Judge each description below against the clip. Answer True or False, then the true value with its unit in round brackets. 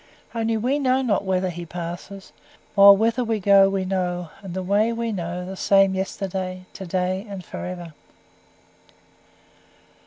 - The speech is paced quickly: False (155 wpm)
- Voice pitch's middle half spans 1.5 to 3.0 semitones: True (2.4 semitones)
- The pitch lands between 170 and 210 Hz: True (190 Hz)